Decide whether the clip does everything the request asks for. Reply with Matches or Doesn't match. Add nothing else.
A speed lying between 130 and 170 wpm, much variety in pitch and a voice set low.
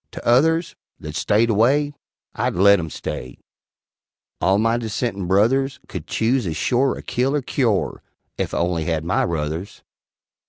Matches